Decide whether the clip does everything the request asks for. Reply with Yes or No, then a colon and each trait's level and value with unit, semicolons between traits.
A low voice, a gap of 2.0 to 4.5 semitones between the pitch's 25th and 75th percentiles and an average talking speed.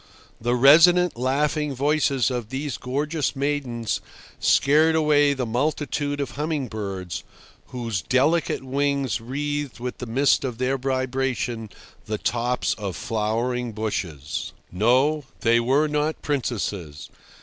No: low, 130 Hz; average, 3.7 semitones; slow, 120 wpm